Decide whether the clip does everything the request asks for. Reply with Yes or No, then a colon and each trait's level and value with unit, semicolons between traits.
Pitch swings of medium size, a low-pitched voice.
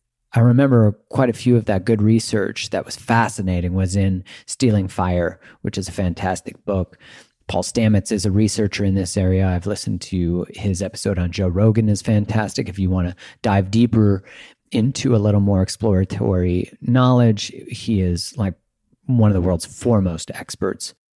Yes: average, 3.4 semitones; low, 100 Hz